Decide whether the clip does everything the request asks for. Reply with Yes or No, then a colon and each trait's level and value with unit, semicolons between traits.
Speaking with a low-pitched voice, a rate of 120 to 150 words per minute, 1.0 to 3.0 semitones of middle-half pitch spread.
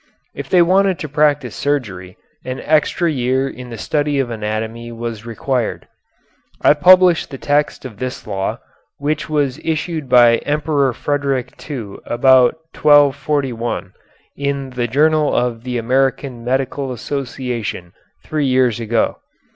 No: low, 130 Hz; slow, 135 wpm; average, 3.7 semitones